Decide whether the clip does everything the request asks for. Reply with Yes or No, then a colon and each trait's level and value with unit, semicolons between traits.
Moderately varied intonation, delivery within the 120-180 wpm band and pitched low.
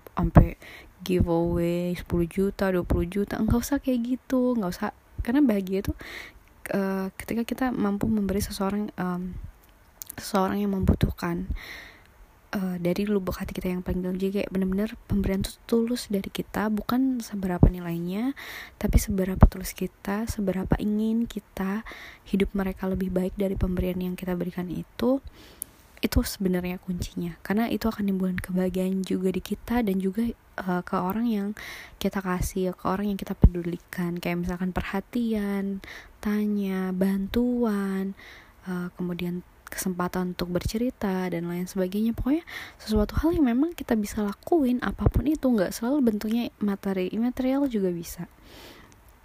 No: average, 3.3 semitones; fast, 140 wpm; high, 195 Hz